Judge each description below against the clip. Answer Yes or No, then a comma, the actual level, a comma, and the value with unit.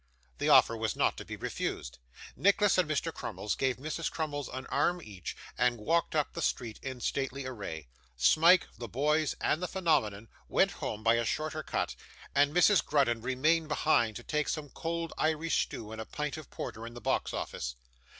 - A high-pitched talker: No, medium, 140 Hz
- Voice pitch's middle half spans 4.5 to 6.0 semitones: Yes, wide, 5.5 semitones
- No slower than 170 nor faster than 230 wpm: Yes, average, 190 wpm